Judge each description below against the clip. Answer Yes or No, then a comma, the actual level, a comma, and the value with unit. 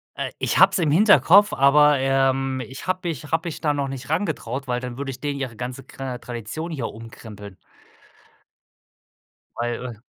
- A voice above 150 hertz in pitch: No, low, 135 Hz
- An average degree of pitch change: Yes, average, 3.6 semitones